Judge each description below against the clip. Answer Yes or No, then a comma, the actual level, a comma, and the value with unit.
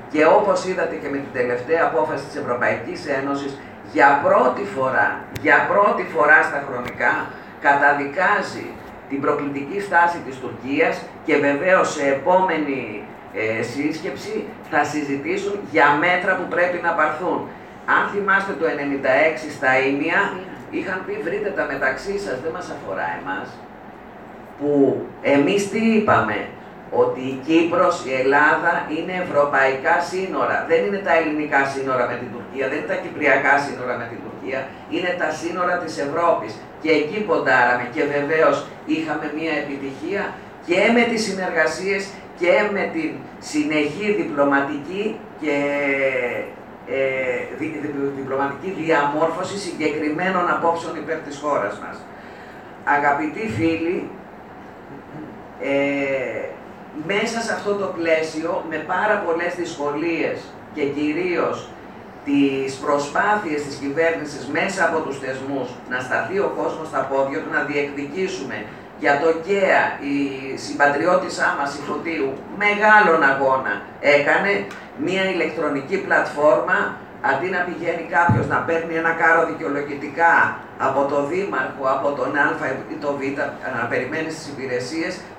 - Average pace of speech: Yes, average, 130 wpm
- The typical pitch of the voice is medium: Yes, medium, 155 Hz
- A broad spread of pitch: No, average, 3.8 semitones